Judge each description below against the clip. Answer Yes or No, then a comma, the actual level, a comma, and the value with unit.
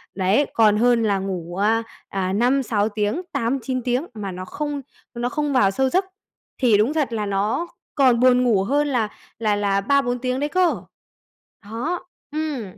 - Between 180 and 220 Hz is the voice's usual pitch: No, high, 235 Hz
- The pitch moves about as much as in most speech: Yes, average, 5.0 semitones